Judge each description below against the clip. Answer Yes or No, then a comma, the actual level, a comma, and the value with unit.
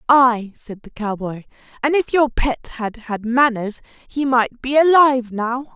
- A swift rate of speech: No, average, 165 wpm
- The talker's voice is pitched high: Yes, high, 245 Hz